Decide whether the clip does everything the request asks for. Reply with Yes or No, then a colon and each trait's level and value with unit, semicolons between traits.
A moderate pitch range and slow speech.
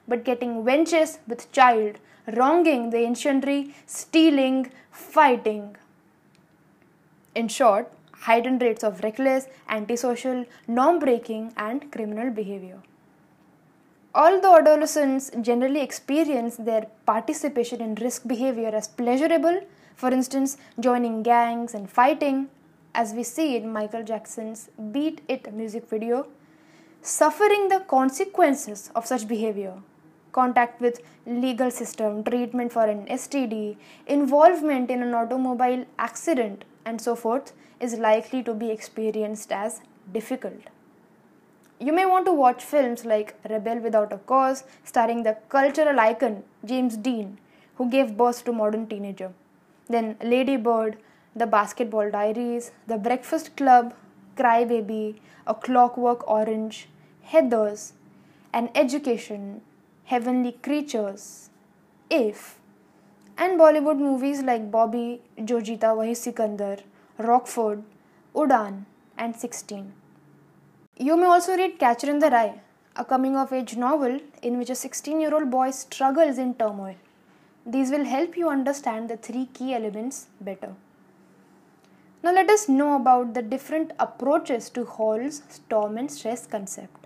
Yes: average, 3.5 semitones; slow, 120 wpm